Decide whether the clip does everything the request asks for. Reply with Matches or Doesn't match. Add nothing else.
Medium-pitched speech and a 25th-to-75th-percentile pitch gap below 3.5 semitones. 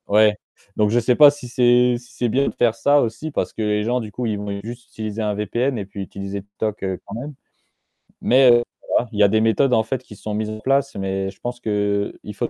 Doesn't match